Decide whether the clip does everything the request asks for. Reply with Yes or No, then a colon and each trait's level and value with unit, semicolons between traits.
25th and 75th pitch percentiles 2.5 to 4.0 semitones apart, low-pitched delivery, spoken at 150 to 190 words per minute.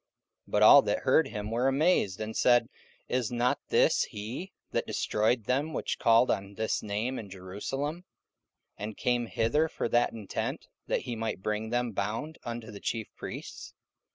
Yes: average, 3.1 semitones; low, 115 Hz; average, 170 wpm